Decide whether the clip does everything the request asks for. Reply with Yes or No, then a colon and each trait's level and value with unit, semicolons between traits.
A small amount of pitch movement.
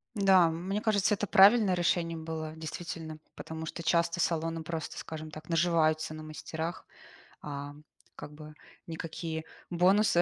Yes: narrow, 2.0 semitones